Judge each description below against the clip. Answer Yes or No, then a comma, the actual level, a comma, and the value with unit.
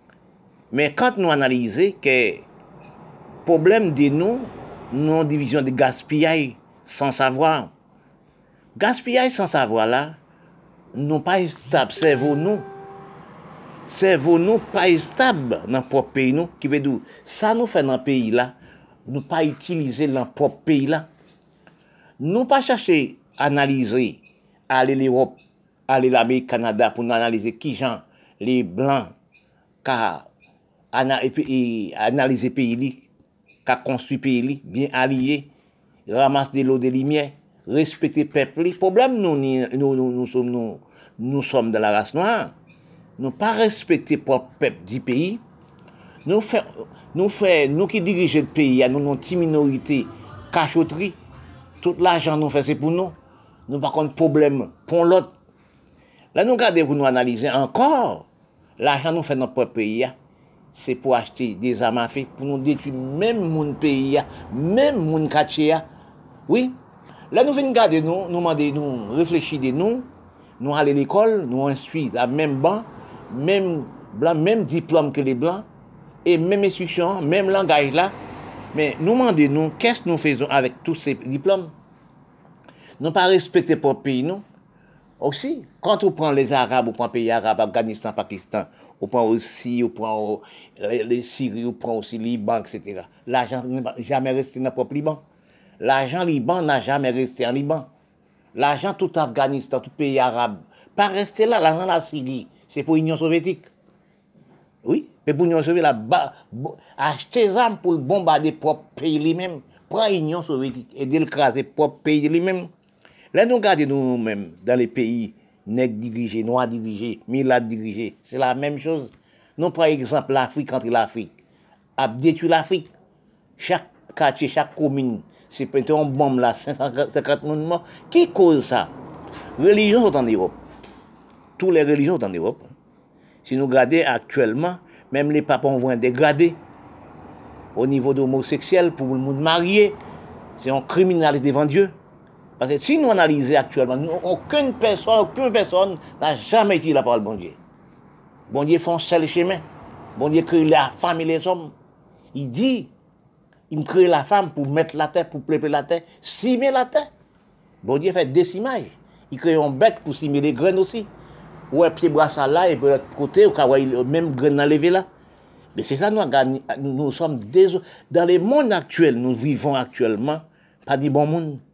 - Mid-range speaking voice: Yes, medium, 150 Hz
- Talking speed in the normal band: Yes, average, 160 wpm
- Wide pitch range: No, average, 4.9 semitones